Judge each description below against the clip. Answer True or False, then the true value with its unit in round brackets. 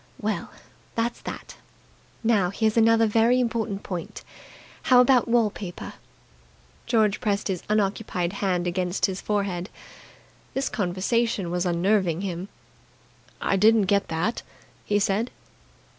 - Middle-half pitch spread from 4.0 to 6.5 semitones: False (3.6 semitones)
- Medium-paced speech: False (120 wpm)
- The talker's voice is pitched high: True (205 Hz)